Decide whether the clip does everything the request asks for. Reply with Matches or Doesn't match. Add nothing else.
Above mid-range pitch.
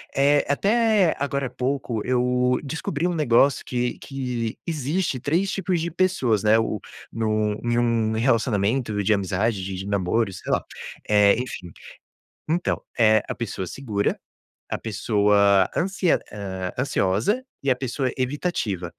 Doesn't match